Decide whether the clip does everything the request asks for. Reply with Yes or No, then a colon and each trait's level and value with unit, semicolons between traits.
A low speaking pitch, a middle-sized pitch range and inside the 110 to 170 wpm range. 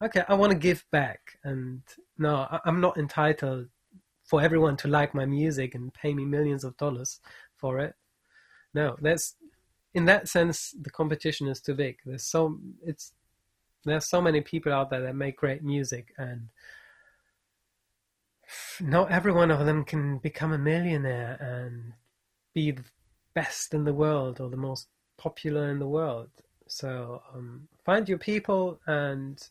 No: medium, 145 Hz; average, 3.9 semitones; average, 160 wpm